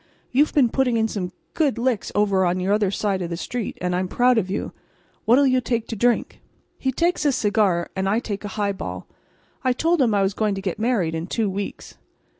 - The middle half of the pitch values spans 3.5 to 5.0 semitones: Yes, average, 4.4 semitones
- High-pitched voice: Yes, high, 215 Hz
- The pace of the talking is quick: Yes, fast, 220 wpm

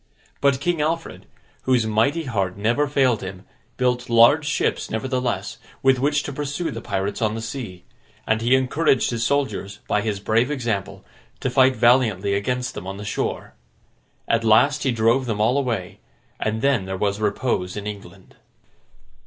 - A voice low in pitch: Yes, low, 115 Hz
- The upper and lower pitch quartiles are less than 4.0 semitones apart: No, average, 4.3 semitones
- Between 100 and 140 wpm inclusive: No, average, 165 wpm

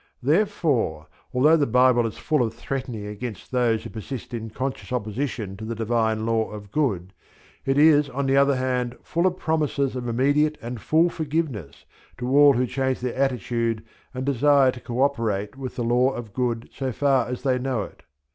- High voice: No, low, 125 Hz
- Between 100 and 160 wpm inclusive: No, average, 185 wpm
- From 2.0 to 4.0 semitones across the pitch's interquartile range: Yes, average, 3.4 semitones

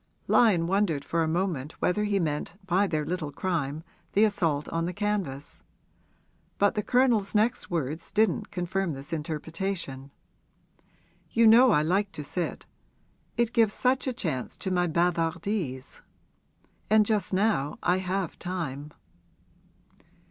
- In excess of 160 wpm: No, slow, 135 wpm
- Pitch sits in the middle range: Yes, medium, 180 Hz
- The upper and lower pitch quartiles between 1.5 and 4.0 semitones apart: No, average, 4.8 semitones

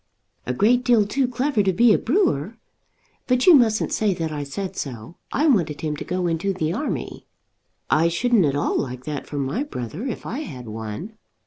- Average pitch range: No, wide, 8.6 semitones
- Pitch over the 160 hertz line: Yes, medium, 185 Hz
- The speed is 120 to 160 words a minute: No, average, 200 wpm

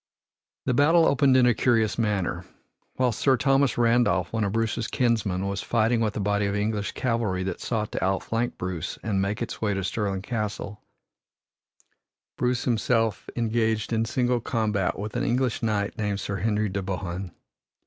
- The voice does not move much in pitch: No, average, 3.1 semitones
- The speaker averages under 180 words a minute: Yes, average, 170 wpm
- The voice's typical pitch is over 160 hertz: No, low, 110 Hz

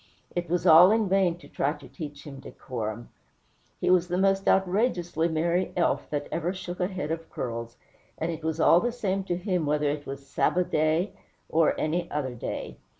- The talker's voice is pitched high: No, medium, 165 Hz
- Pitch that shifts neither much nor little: Yes, average, 3.5 semitones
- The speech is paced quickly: No, average, 195 wpm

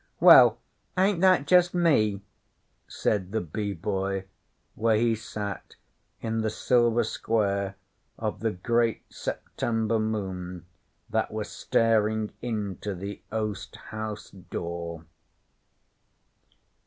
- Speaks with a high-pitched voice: No, low, 110 Hz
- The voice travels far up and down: No, narrow, 2.6 semitones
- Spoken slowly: Yes, slow, 105 wpm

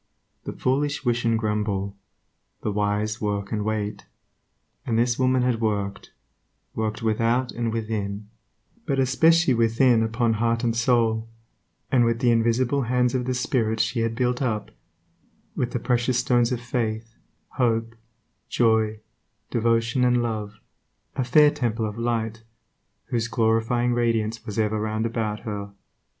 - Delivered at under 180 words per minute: Yes, average, 140 wpm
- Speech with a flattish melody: Yes, narrow, 2.0 semitones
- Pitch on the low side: Yes, low, 115 Hz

